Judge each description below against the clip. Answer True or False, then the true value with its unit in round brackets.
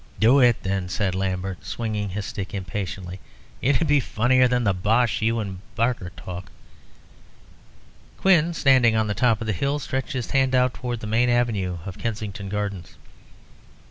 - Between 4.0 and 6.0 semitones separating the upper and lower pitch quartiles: True (4.3 semitones)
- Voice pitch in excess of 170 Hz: False (110 Hz)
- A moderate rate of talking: True (170 wpm)